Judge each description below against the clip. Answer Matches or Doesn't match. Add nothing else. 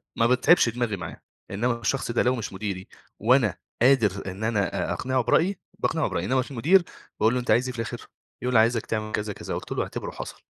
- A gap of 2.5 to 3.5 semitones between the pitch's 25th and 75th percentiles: Matches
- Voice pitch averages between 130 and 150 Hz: Doesn't match